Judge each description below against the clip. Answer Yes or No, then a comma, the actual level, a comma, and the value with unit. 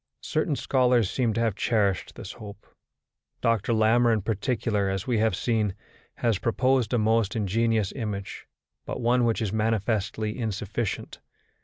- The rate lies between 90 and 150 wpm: Yes, average, 145 wpm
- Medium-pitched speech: No, low, 110 Hz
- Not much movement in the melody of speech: Yes, narrow, 2.2 semitones